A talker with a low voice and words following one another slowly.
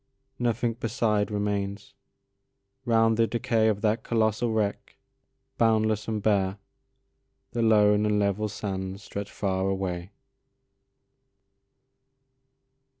Yes: low, 105 Hz; slow, 90 wpm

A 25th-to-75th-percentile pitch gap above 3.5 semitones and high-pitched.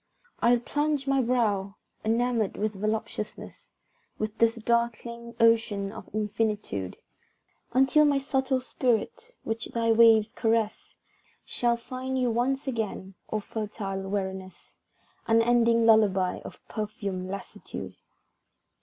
No: narrow, 2.5 semitones; high, 225 Hz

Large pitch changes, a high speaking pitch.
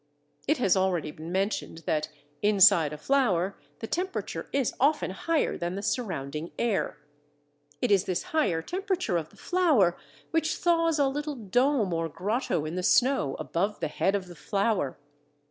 Yes: wide, 8.3 semitones; high, 200 Hz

